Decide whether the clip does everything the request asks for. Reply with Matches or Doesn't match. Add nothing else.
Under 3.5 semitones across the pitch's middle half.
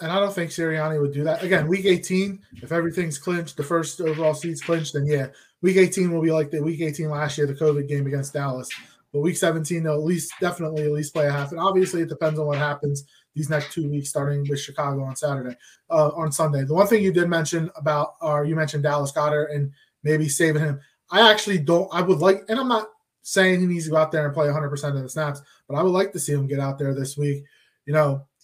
Matches